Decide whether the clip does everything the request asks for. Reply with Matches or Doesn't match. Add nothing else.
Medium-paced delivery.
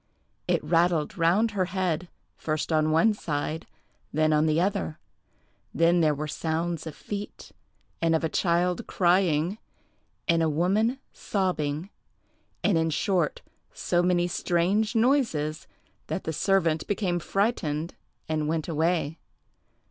Doesn't match